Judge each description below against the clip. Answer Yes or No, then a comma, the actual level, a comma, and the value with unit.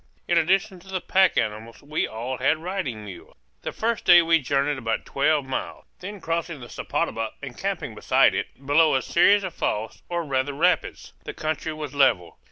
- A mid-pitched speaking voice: Yes, medium, 150 Hz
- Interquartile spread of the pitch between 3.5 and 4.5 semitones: No, average, 4.9 semitones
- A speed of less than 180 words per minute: No, average, 185 wpm